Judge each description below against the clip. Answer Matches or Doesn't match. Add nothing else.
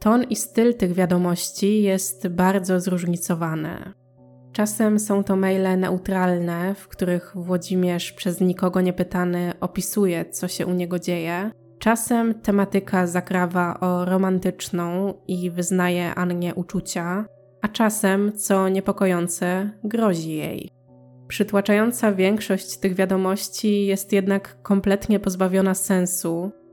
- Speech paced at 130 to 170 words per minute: Doesn't match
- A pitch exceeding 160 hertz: Matches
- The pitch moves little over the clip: Matches